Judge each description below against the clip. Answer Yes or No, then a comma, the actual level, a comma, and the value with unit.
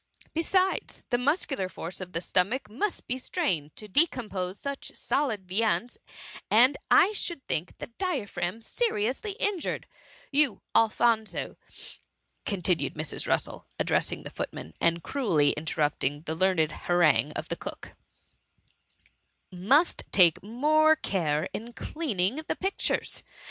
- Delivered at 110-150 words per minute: Yes, slow, 135 wpm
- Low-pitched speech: No, high, 215 Hz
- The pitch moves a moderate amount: No, wide, 8.4 semitones